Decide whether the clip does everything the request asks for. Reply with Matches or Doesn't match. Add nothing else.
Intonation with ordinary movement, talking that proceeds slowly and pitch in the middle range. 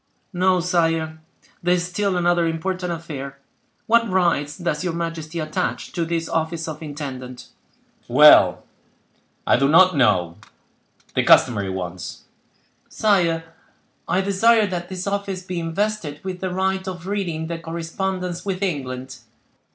Matches